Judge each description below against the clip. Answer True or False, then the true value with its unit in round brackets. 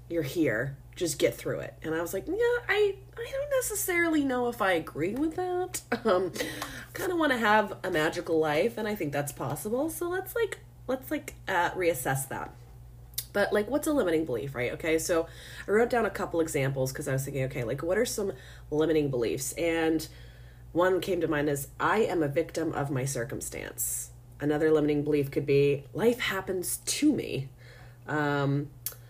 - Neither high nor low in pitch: True (160 Hz)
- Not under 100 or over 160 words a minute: False (190 wpm)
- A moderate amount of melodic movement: False (8.4 semitones)